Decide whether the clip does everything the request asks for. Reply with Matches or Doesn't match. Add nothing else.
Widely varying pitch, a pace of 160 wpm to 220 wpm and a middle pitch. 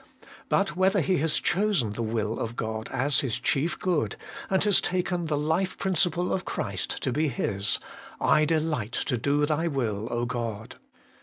Matches